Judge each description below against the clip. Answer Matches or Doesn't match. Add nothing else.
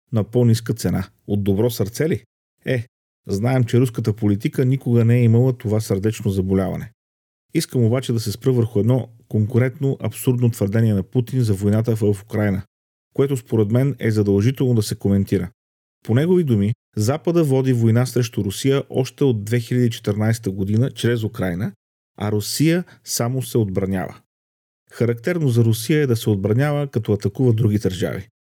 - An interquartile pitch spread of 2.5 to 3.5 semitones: Doesn't match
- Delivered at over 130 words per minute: Matches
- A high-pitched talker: Doesn't match